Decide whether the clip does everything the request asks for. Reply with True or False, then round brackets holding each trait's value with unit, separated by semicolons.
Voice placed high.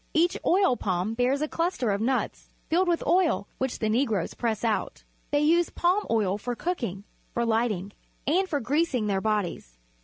True (245 Hz)